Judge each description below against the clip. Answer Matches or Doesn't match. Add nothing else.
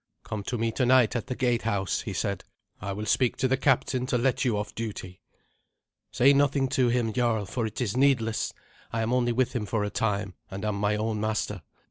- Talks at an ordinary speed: Doesn't match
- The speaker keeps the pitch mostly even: Doesn't match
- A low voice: Matches